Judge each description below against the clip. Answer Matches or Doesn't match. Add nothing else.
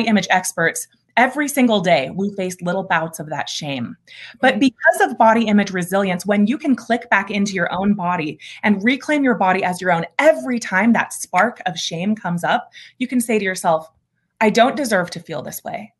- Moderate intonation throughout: Matches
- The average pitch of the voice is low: Doesn't match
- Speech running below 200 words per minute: Doesn't match